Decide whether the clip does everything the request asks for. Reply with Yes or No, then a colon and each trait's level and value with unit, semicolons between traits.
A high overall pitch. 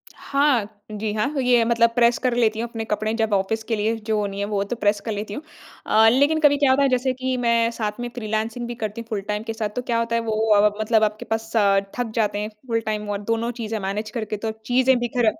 Yes: high, 225 Hz